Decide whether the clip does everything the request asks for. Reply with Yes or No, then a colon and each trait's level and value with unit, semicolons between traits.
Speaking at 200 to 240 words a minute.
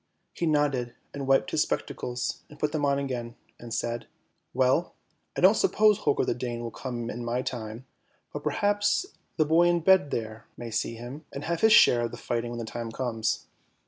Yes: fast, 205 wpm